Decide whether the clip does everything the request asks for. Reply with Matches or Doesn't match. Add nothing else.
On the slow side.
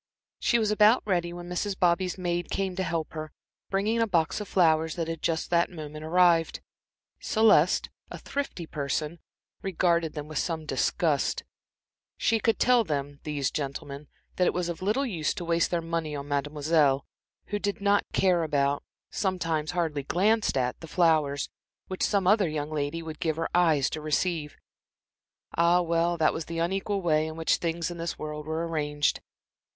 Doesn't match